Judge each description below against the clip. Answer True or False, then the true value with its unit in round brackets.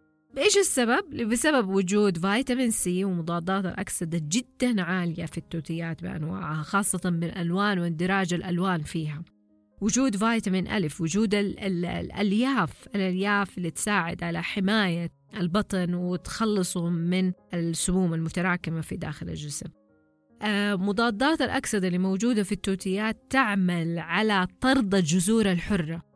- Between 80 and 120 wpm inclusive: True (110 wpm)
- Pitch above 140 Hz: True (185 Hz)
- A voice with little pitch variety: False (3.5 semitones)